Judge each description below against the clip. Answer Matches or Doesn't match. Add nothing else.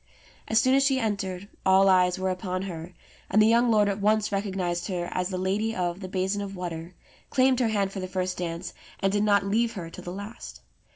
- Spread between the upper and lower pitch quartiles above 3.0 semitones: Doesn't match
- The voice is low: Doesn't match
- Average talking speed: Doesn't match